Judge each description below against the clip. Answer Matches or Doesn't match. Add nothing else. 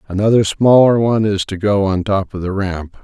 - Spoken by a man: Matches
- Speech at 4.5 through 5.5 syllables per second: Matches